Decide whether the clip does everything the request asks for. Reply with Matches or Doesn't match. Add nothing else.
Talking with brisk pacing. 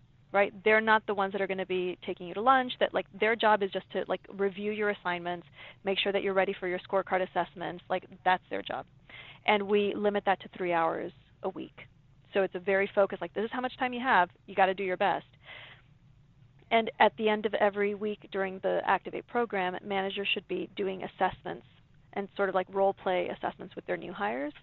Matches